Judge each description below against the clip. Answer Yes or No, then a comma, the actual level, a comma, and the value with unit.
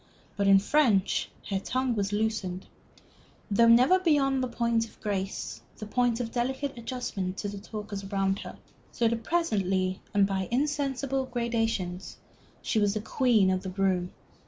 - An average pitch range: Yes, average, 4.3 semitones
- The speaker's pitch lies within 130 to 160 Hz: No, high, 220 Hz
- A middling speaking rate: Yes, average, 160 wpm